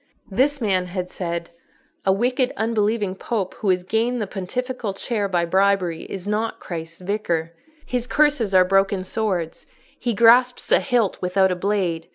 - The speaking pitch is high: Yes, high, 200 Hz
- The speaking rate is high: No, average, 160 wpm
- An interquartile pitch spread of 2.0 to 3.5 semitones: No, average, 4.1 semitones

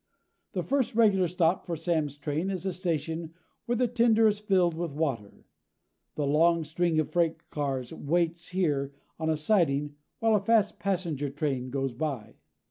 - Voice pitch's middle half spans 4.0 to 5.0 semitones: Yes, average, 4.5 semitones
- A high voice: No, medium, 165 Hz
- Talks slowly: No, average, 165 wpm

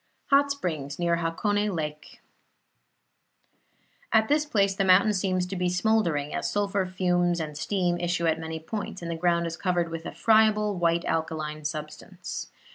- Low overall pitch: No, medium, 175 Hz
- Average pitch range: Yes, average, 3.7 semitones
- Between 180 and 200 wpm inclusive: No, average, 160 wpm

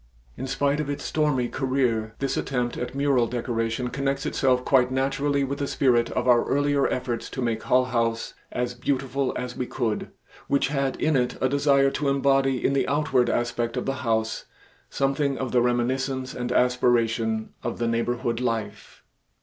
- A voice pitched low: Yes, low, 130 Hz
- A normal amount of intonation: No, narrow, 2.3 semitones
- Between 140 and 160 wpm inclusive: No, average, 175 wpm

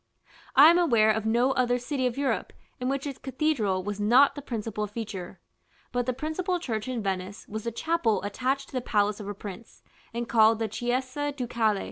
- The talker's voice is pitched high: Yes, high, 240 Hz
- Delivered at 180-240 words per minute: Yes, average, 195 wpm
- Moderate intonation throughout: Yes, average, 4.0 semitones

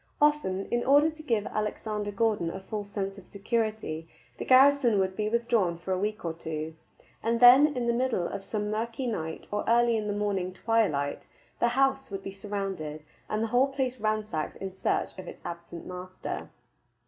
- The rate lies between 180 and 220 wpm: Yes, average, 185 wpm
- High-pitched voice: Yes, high, 210 Hz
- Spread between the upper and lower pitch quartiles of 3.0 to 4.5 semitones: Yes, average, 4.0 semitones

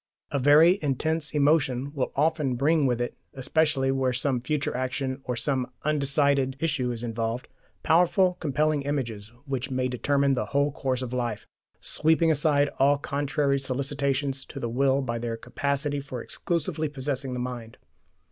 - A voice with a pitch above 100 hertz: Yes, medium, 140 Hz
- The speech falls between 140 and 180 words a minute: Yes, average, 155 wpm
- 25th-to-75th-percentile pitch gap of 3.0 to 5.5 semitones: No, narrow, 2.5 semitones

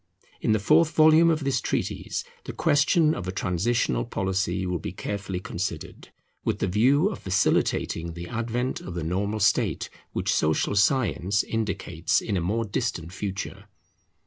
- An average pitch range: Yes, average, 4.8 semitones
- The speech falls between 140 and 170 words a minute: Yes, average, 155 wpm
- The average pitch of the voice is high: No, low, 100 Hz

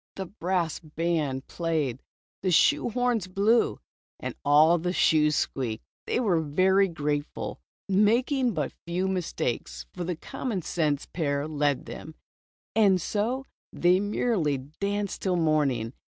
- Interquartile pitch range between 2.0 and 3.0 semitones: No, average, 5.0 semitones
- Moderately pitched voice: Yes, medium, 170 Hz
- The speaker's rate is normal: No, slow, 130 wpm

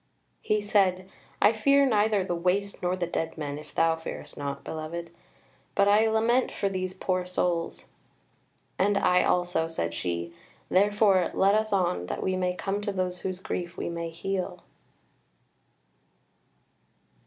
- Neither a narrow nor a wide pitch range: Yes, average, 3.3 semitones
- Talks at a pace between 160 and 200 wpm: No, average, 150 wpm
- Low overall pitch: No, medium, 185 Hz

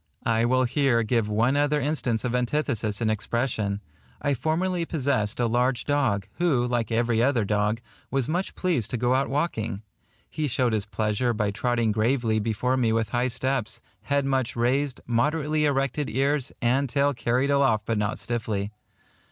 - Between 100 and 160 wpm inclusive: No, average, 170 wpm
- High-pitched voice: No, low, 125 Hz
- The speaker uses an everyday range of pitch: Yes, average, 3.8 semitones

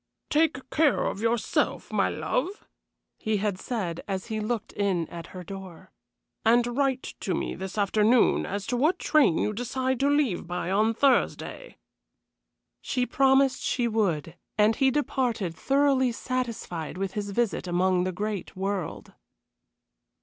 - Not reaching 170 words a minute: Yes, average, 145 wpm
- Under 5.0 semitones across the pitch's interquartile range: No, average, 5.3 semitones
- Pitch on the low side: No, high, 220 Hz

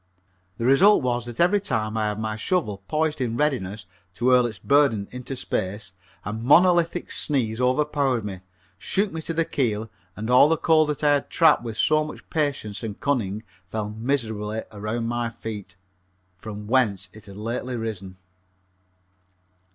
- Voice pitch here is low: Yes, low, 120 Hz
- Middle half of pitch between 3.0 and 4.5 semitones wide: No, average, 5.3 semitones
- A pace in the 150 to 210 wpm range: Yes, average, 165 wpm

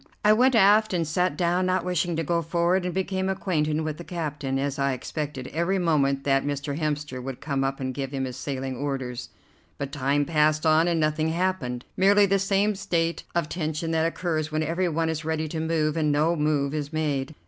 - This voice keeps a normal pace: No, fast, 210 wpm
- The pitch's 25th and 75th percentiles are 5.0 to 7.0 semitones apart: No, average, 3.4 semitones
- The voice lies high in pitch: No, medium, 155 Hz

